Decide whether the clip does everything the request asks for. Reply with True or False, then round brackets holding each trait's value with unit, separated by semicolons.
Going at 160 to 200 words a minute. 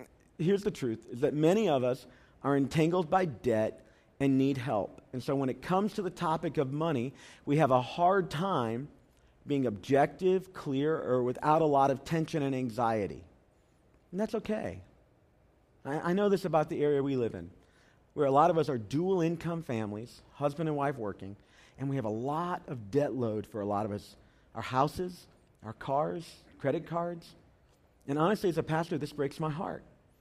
True (190 wpm)